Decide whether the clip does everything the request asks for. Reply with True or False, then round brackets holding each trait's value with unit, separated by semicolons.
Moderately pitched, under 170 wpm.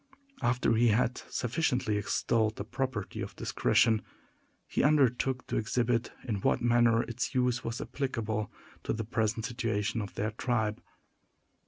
False (115 Hz; 140 wpm)